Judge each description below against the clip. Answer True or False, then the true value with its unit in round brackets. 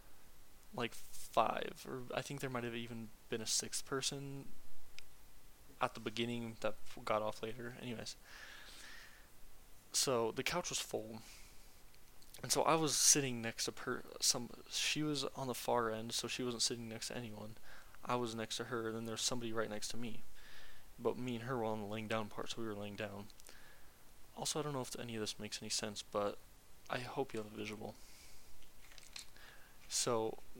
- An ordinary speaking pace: True (185 wpm)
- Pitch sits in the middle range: False (115 Hz)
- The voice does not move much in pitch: True (2.3 semitones)